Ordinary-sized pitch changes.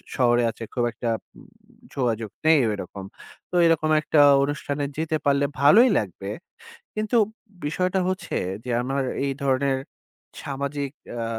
Yes: average, 3.6 semitones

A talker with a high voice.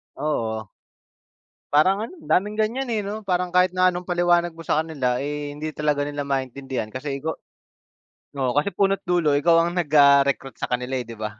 No: medium, 150 Hz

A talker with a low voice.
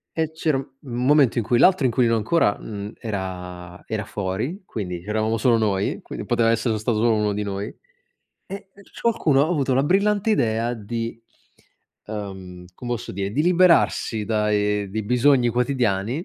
Yes: low, 115 Hz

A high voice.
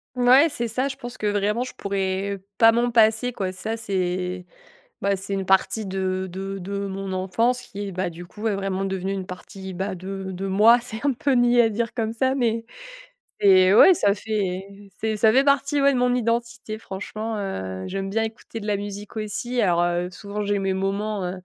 Yes: high, 205 Hz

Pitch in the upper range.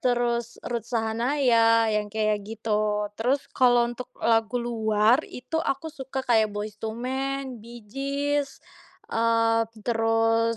Yes: high, 230 Hz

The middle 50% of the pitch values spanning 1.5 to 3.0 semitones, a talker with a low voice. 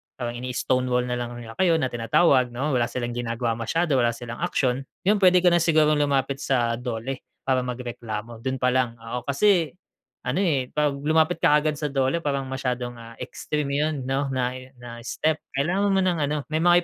No: average, 3.9 semitones; low, 130 Hz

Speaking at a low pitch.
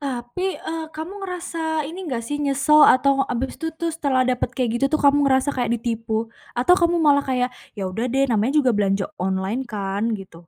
No: very high, 260 Hz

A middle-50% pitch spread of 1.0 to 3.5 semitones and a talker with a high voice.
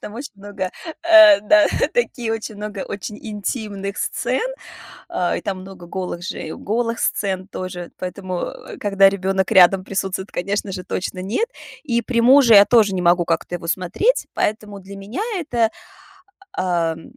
Yes: average, 2.8 semitones; high, 195 Hz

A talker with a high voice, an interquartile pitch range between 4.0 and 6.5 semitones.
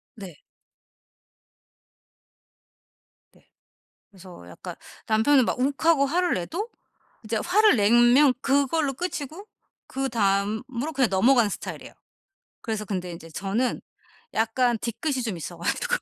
Yes: high, 240 Hz; wide, 5.8 semitones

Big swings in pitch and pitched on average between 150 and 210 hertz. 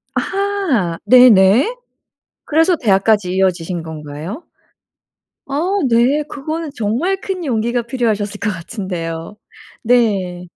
No: wide, 7.2 semitones; high, 225 Hz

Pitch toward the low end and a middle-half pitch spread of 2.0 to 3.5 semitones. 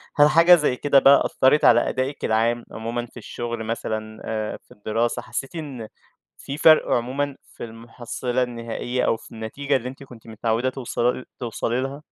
Yes: low, 120 Hz; average, 3.0 semitones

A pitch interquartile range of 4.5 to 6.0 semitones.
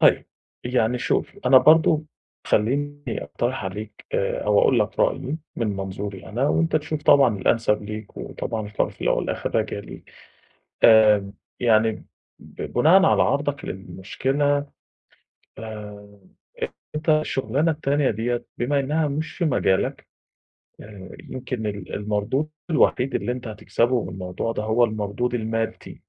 Yes: wide, 5.4 semitones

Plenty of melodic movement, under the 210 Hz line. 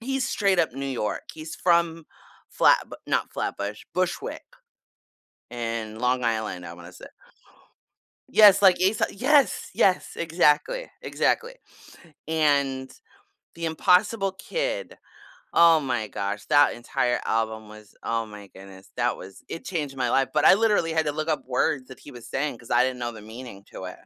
Yes: wide, 7.4 semitones; low, 135 Hz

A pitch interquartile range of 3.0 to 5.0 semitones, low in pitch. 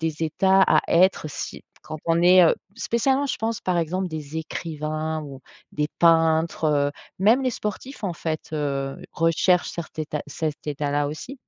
No: average, 3.4 semitones; medium, 160 Hz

